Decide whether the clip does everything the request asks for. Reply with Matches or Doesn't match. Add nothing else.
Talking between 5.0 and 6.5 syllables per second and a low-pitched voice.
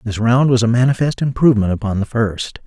Matches